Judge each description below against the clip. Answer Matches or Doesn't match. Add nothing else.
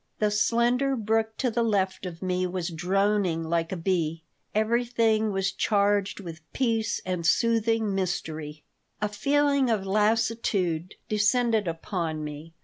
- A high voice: Matches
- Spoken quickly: Doesn't match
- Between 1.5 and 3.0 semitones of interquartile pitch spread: Doesn't match